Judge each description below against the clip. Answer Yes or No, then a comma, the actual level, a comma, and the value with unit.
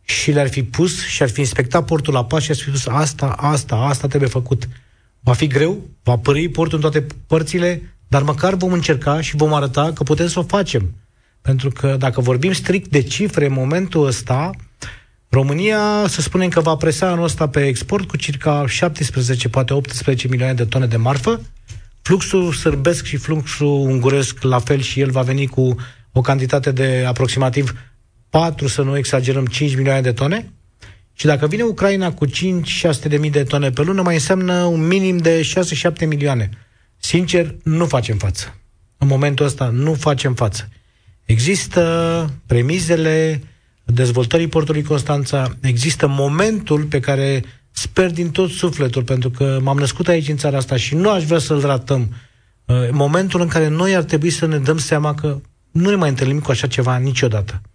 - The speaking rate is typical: No, fast, 175 wpm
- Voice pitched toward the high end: No, medium, 140 Hz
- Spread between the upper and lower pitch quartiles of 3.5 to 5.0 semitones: Yes, average, 4.0 semitones